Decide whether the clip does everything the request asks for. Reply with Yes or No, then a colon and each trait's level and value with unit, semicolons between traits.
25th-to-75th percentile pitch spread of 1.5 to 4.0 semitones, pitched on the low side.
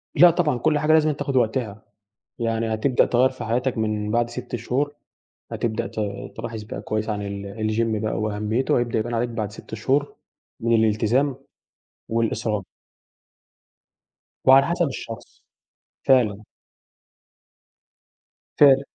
Yes: average, 3.4 semitones; low, 115 Hz